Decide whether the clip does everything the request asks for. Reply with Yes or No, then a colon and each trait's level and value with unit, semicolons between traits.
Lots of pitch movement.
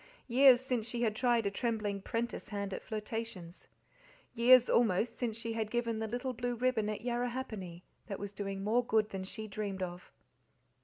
No: average, 3.0 semitones